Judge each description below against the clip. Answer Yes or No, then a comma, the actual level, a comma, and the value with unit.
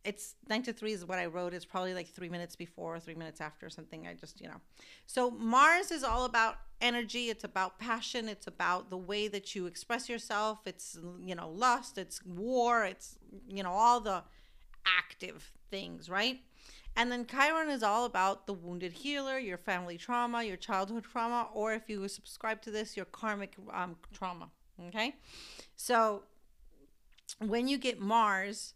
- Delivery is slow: No, average, 175 wpm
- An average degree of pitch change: Yes, average, 4.2 semitones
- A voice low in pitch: No, high, 210 Hz